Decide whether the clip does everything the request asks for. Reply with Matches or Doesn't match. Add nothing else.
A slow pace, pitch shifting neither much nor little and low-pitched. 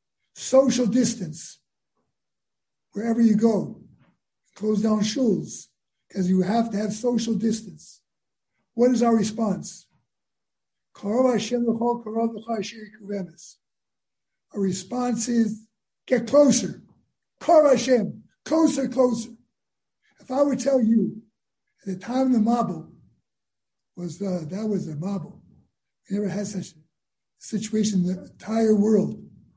Doesn't match